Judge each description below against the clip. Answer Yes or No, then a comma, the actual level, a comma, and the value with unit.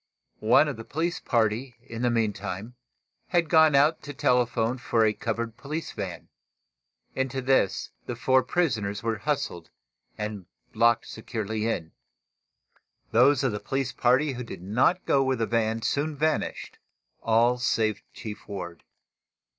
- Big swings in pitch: No, average, 3.7 semitones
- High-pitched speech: No, low, 120 Hz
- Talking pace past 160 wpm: No, average, 145 wpm